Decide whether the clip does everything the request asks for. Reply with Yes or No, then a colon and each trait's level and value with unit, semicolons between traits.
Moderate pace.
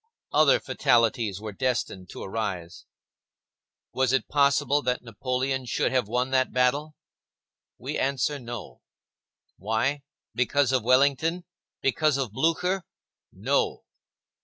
No: slow, 110 wpm